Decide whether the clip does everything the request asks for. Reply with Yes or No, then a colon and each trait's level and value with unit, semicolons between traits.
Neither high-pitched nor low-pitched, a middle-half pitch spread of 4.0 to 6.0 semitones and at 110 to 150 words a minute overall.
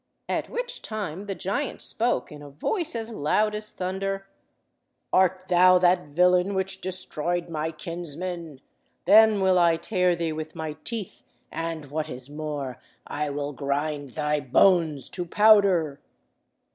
Yes: medium, 175 Hz; average, 4.4 semitones; average, 145 wpm